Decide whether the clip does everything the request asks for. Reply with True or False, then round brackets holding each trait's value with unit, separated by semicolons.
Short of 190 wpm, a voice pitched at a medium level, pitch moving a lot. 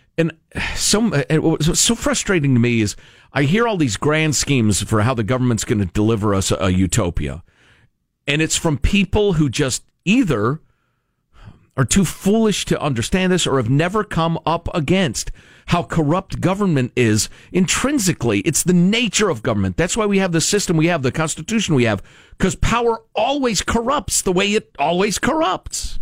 True (170 wpm; 160 Hz; 7.7 semitones)